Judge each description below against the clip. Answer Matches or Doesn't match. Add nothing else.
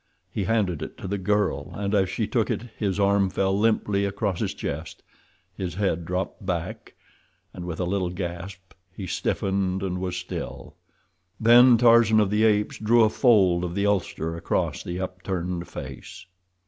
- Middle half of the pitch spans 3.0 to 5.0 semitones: Doesn't match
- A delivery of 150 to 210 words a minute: Matches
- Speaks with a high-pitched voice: Doesn't match